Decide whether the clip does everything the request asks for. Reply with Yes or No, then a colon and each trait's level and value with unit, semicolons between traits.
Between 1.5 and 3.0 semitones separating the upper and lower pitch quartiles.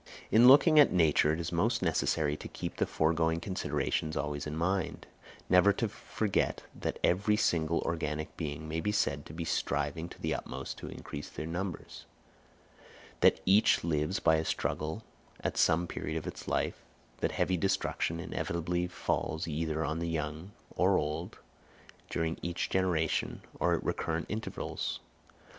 Yes: average, 2.7 semitones